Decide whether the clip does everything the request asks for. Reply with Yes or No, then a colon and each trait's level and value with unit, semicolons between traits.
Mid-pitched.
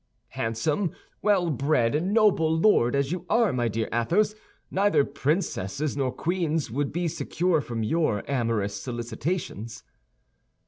Yes: medium, 145 Hz